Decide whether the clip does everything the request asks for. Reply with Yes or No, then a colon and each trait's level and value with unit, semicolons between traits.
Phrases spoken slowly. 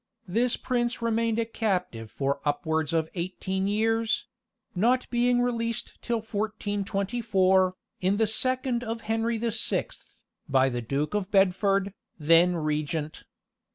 Yes: slow, 125 wpm